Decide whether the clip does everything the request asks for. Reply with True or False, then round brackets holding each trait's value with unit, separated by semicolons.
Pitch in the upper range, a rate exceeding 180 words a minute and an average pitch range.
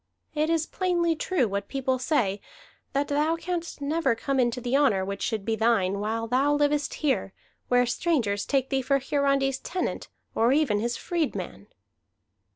False (270 Hz; 165 wpm; 4.6 semitones)